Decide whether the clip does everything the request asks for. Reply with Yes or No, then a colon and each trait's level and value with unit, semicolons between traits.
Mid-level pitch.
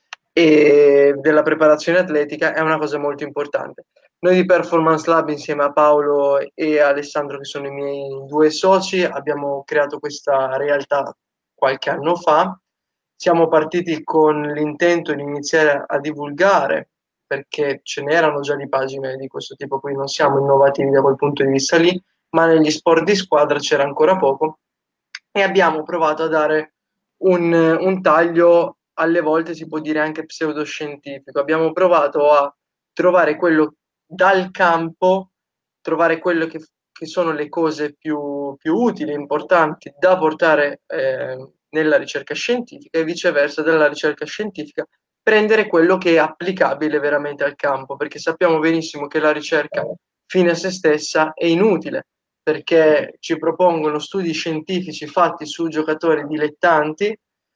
Yes: medium, 155 Hz